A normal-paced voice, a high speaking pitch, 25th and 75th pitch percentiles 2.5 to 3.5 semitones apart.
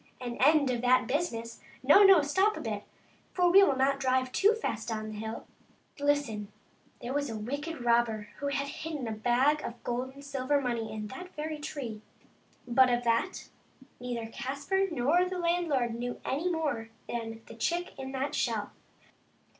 No: average, 175 wpm; very high, 260 Hz; average, 4.3 semitones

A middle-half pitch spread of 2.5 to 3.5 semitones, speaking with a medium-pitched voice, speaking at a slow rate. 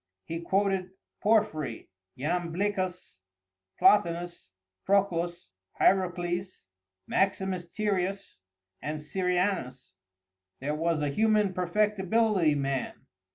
Yes: average, 3.1 semitones; medium, 180 Hz; slow, 75 wpm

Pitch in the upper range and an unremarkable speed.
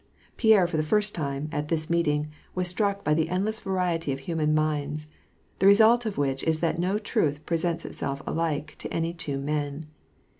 No: medium, 165 Hz; average, 185 wpm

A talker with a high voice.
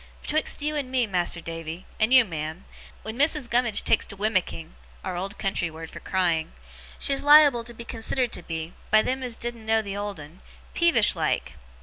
Yes: high, 215 Hz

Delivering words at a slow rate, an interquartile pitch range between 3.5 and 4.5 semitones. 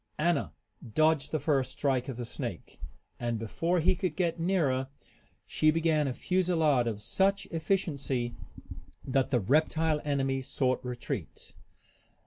Yes: slow, 130 wpm; average, 4.2 semitones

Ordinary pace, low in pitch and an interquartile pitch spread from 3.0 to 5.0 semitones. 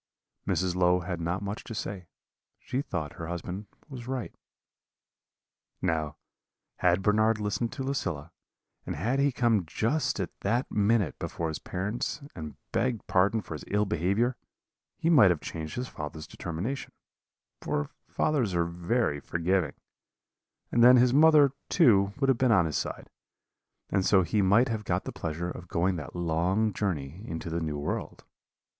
No: average, 160 wpm; very low, 95 Hz; wide, 5.6 semitones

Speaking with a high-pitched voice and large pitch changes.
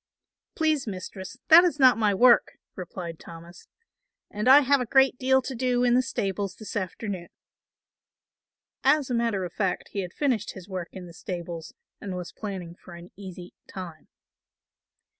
Yes: high, 200 Hz; wide, 5.8 semitones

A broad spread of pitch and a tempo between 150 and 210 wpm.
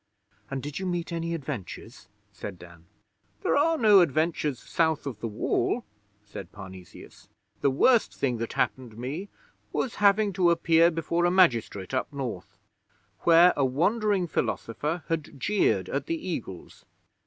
No: wide, 7.0 semitones; average, 140 wpm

